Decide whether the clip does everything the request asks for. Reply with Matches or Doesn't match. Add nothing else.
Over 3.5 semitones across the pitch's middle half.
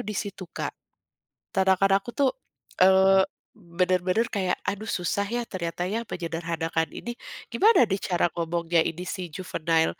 Doesn't match